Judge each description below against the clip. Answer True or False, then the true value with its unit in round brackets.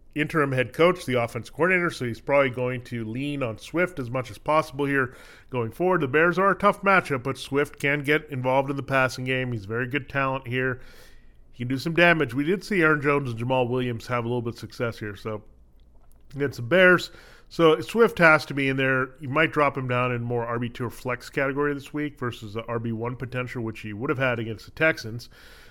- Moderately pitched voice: False (130 Hz)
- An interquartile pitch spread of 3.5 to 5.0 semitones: True (3.8 semitones)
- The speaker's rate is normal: False (225 wpm)